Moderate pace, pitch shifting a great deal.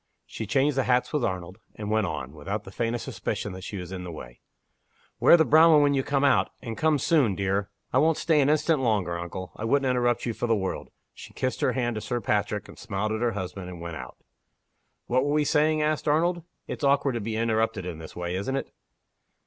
No: fast, 235 wpm; wide, 6.5 semitones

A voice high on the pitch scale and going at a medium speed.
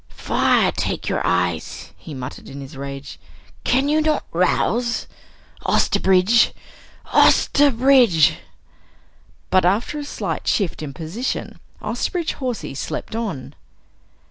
No: high, 200 Hz; slow, 110 wpm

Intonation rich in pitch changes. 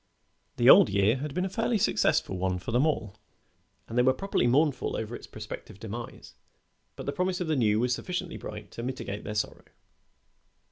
Yes: wide, 6.9 semitones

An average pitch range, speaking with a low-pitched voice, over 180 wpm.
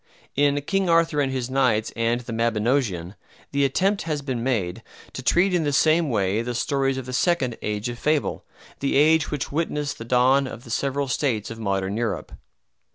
Yes: average, 4.1 semitones; low, 130 Hz; average, 190 wpm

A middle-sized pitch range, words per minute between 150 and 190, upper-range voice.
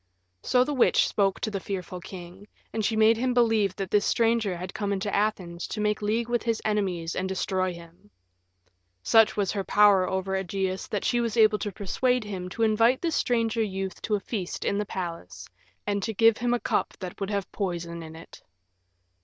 No: average, 3.2 semitones; fast, 205 wpm; high, 205 Hz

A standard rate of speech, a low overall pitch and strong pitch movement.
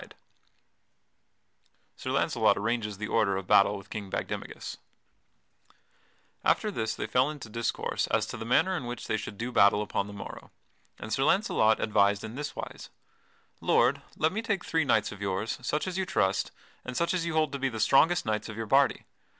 Yes: average, 190 wpm; low, 115 Hz; wide, 6.1 semitones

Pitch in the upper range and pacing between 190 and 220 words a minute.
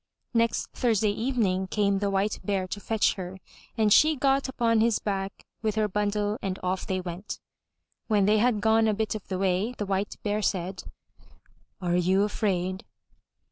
No: high, 205 Hz; average, 175 wpm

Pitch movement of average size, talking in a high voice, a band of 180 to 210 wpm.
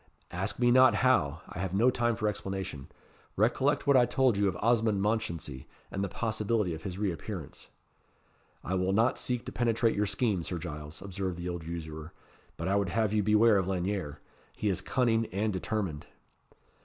No: average, 4.3 semitones; low, 100 Hz; average, 185 wpm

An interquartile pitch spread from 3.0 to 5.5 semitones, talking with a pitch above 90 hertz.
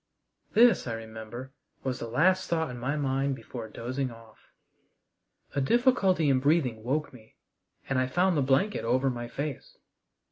Yes: average, 4.3 semitones; low, 135 Hz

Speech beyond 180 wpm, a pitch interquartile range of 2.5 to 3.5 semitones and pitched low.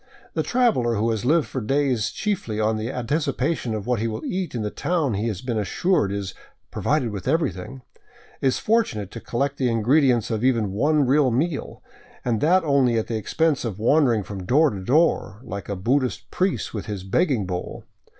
No: average, 190 wpm; wide, 5.4 semitones; low, 120 Hz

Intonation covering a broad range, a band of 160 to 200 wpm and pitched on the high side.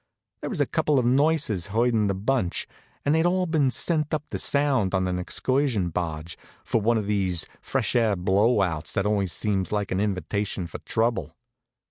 No: wide, 5.9 semitones; average, 185 wpm; low, 105 Hz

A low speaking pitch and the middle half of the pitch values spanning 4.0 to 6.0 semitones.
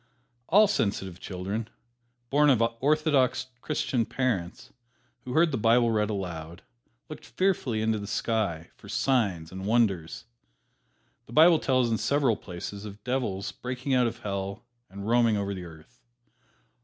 Yes: low, 110 Hz; average, 4.7 semitones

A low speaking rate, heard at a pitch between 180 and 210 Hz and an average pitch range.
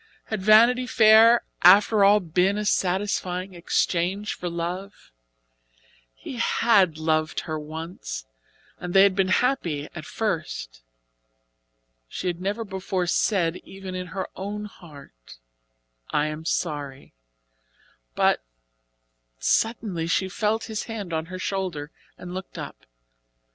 Yes: slow, 120 wpm; medium, 185 Hz; average, 4.0 semitones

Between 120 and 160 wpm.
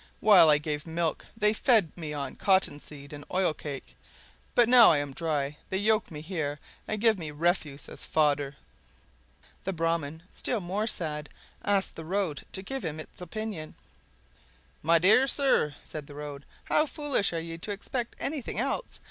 No: average, 170 wpm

